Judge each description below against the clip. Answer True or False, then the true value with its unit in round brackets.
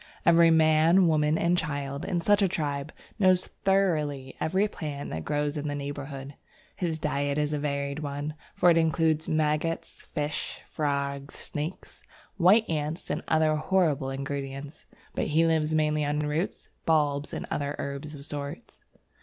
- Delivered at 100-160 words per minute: True (150 wpm)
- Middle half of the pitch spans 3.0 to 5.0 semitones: False (2.4 semitones)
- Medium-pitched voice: True (150 Hz)